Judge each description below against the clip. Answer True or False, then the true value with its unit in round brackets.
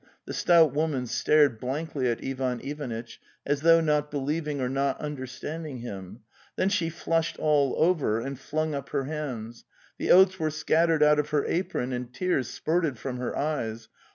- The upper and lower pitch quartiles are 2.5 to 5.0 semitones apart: True (3.7 semitones)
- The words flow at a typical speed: True (170 wpm)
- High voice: False (145 Hz)